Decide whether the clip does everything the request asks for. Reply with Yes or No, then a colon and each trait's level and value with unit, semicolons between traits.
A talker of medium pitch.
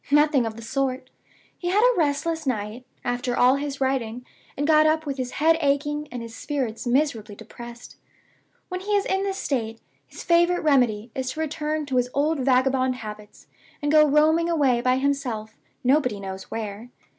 No: very high, 270 Hz